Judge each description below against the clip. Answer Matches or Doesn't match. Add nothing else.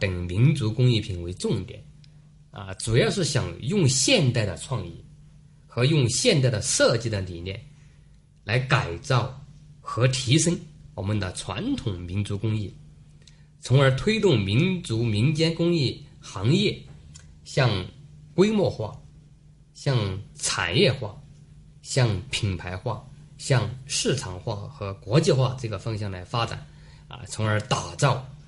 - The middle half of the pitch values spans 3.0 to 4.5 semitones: Doesn't match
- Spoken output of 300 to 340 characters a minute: Doesn't match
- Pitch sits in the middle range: Doesn't match